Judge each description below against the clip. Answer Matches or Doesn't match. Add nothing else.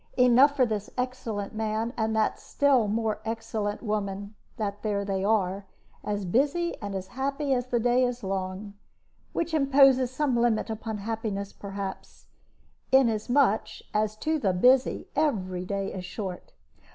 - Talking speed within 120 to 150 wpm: Matches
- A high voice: Matches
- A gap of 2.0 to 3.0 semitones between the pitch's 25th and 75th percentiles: Doesn't match